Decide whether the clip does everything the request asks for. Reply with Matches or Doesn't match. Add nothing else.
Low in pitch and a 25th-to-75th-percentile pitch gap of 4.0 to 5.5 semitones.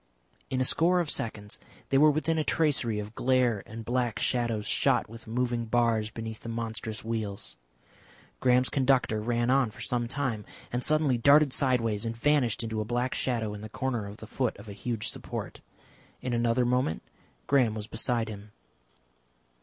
Doesn't match